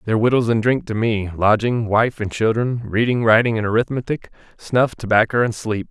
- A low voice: Yes, low, 110 Hz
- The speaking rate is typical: Yes, average, 150 wpm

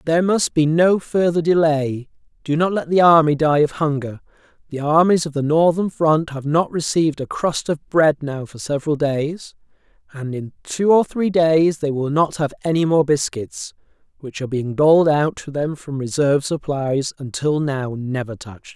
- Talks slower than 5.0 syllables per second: Yes, 4.8 syllables/s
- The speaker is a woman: No, male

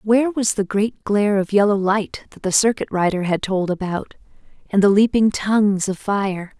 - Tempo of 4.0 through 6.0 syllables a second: Yes, 4.9 syllables/s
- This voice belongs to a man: No, female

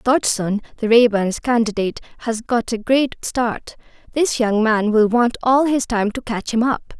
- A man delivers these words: No, female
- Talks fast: No, average, 180 wpm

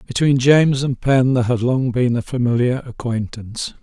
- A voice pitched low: Yes, low, 125 Hz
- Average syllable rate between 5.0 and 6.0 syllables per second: Yes, 5.3 syllables/s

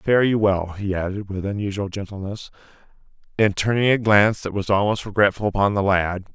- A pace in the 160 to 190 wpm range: Yes, average, 180 wpm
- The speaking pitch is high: No, low, 100 Hz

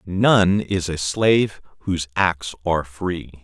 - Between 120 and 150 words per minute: Yes, average, 140 wpm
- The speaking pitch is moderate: No, very low, 90 Hz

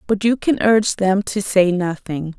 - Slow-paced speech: No, average, 200 wpm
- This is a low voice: No, high, 200 Hz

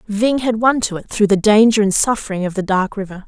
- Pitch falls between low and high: No, high, 210 Hz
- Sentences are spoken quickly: Yes, fast, 255 wpm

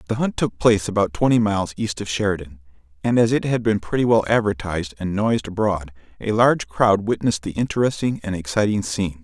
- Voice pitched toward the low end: Yes, low, 105 Hz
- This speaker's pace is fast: No, average, 195 wpm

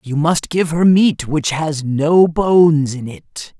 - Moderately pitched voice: Yes, medium, 155 Hz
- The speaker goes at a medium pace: Yes, average, 185 wpm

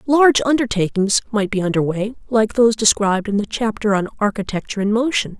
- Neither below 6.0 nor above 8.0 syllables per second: Yes, 6.1 syllables/s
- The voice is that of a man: No, female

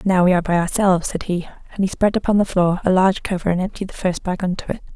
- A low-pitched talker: No, medium, 185 Hz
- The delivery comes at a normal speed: No, fast, 280 wpm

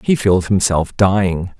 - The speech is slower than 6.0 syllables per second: Yes, 4.1 syllables/s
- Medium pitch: No, very low, 95 Hz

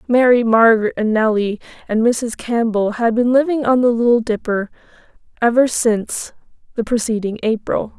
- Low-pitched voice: No, high, 230 Hz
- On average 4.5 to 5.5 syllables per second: Yes, 5.1 syllables/s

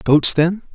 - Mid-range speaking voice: Yes, medium, 170 Hz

